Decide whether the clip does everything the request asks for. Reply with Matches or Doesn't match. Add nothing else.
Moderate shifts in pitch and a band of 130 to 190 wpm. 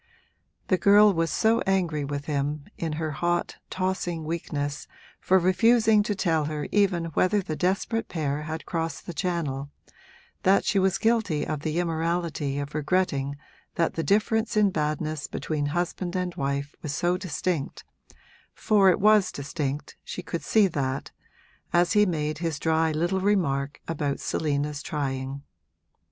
Matches